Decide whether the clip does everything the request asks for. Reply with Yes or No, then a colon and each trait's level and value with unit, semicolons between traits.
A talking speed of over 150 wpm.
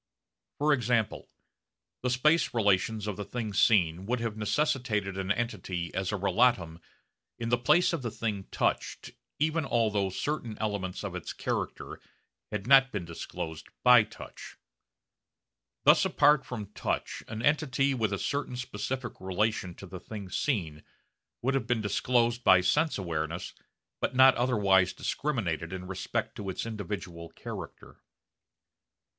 No: average, 145 wpm